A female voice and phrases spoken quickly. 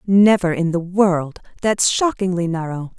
No: female; average, 140 wpm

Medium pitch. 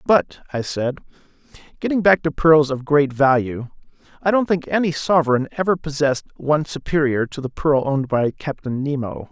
Yes: medium, 145 Hz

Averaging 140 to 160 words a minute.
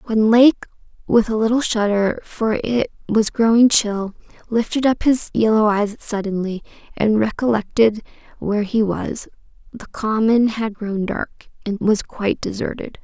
Yes: average, 145 wpm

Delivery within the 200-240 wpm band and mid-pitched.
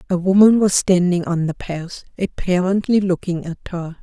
No: average, 165 wpm; medium, 180 Hz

